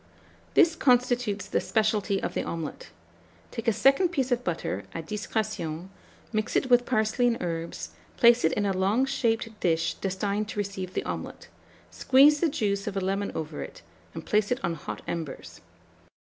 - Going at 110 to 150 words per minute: No, average, 175 wpm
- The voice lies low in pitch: No, high, 210 Hz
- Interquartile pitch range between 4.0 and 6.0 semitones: Yes, average, 4.8 semitones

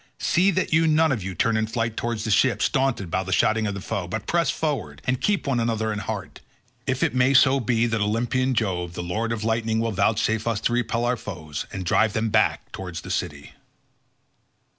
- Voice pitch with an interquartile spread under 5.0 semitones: Yes, average, 3.9 semitones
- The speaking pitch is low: Yes, low, 110 Hz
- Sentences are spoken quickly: Yes, fast, 220 wpm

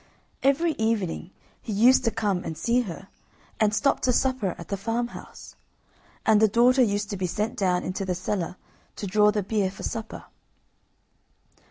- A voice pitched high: Yes, high, 210 Hz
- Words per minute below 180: Yes, average, 170 wpm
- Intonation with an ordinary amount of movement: Yes, average, 3.5 semitones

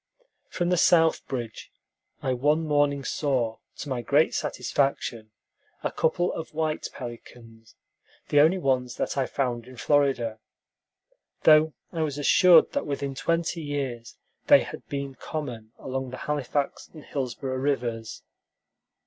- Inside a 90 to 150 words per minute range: Yes, slow, 135 wpm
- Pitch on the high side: No, medium, 140 Hz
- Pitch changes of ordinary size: Yes, average, 3.7 semitones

